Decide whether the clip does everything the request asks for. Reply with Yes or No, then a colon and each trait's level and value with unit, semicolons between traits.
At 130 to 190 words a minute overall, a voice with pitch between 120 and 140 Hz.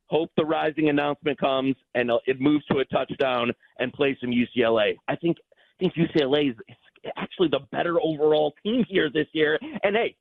No: average, 180 wpm; medium, 150 Hz